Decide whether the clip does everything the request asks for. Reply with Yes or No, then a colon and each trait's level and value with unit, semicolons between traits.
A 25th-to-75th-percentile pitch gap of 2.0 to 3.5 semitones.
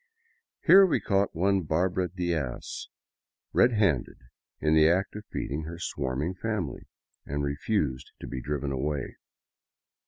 No: average, 5.1 semitones